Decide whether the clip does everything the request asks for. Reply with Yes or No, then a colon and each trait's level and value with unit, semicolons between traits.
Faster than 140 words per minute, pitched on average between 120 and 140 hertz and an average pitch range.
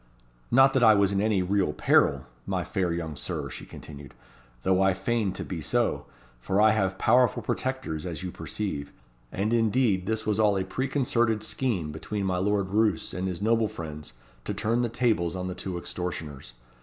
No: average, 185 wpm; low, 100 Hz; average, 3.7 semitones